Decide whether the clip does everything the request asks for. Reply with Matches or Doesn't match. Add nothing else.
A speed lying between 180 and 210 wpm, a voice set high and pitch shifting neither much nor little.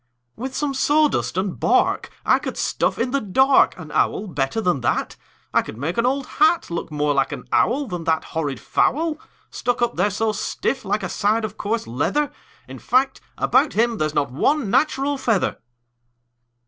Doesn't match